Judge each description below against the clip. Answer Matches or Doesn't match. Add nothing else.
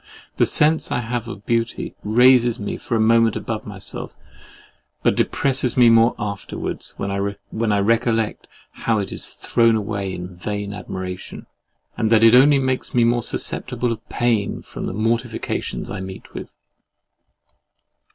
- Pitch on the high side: Doesn't match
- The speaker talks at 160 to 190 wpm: Doesn't match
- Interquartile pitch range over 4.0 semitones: Doesn't match